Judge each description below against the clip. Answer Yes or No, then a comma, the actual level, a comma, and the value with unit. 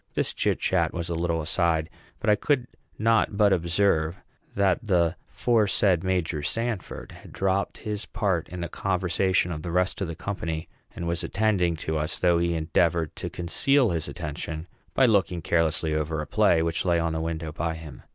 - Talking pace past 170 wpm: Yes, average, 180 wpm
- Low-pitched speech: Yes, very low, 85 Hz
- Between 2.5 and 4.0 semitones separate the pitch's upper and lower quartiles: Yes, average, 3.2 semitones